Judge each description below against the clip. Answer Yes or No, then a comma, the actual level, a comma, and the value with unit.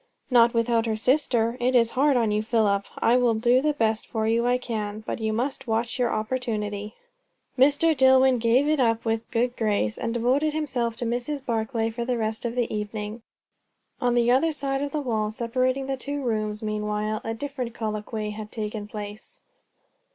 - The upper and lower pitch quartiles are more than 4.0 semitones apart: No, average, 2.8 semitones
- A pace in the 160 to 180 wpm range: No, average, 190 wpm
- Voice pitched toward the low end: No, high, 230 Hz